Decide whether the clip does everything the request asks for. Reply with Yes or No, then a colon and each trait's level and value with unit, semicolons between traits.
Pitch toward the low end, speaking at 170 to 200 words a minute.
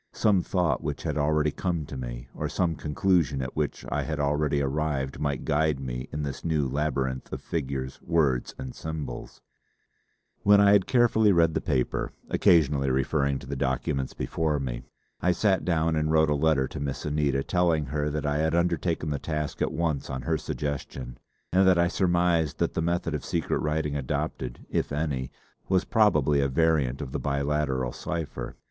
Yes: very low, 75 Hz; average, 190 wpm